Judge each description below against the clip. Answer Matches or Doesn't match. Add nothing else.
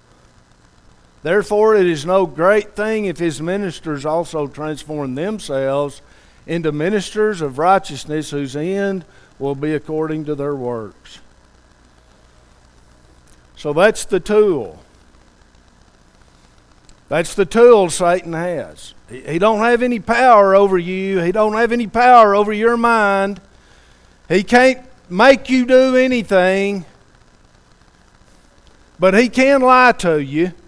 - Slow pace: Matches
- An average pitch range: Doesn't match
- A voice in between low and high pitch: Matches